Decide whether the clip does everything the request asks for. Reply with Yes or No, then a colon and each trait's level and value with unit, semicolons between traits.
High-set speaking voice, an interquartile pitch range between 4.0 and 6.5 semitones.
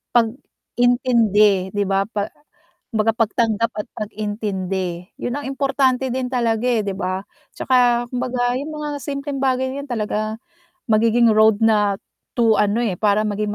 No: high, 225 Hz; average, 3.2 semitones